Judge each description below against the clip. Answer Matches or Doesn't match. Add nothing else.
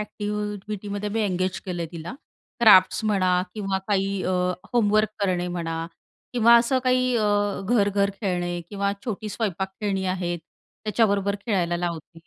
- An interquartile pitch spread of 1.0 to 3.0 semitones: Matches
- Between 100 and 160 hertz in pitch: Doesn't match